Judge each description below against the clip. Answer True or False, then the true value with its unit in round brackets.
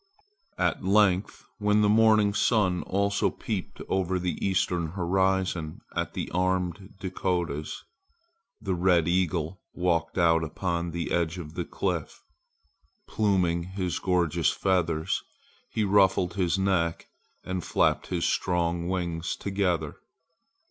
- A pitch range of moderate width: False (2.2 semitones)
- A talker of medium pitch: False (90 Hz)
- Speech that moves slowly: True (120 wpm)